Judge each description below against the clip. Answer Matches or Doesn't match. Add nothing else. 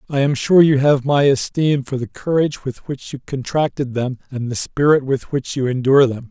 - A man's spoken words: Matches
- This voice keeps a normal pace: Doesn't match